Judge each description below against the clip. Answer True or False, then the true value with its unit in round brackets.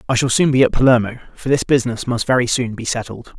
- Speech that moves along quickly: True (250 wpm)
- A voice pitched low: True (125 Hz)